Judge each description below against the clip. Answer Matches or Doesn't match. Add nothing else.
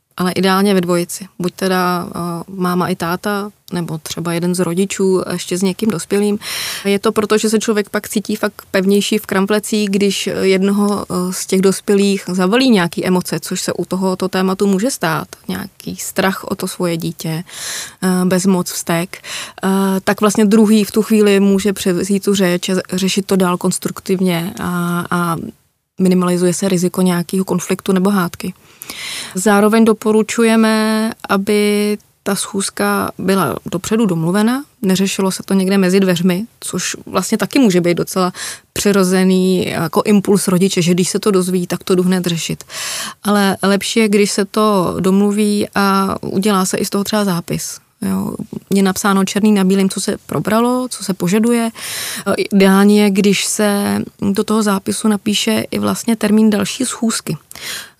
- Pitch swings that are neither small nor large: Doesn't match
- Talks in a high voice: Matches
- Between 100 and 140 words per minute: Doesn't match